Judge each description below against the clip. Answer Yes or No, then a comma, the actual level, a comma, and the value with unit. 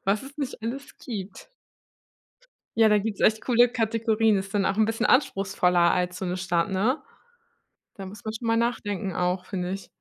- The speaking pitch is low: No, high, 210 Hz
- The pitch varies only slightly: No, average, 3.2 semitones